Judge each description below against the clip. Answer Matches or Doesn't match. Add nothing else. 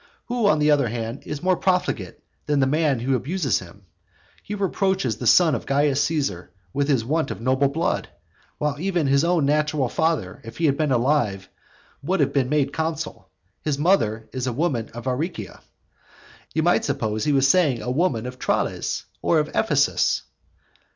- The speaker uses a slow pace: Doesn't match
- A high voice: Doesn't match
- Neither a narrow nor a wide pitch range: Matches